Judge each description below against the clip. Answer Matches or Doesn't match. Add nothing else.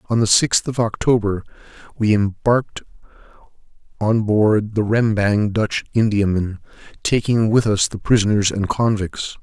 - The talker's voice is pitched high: Doesn't match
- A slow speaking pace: Matches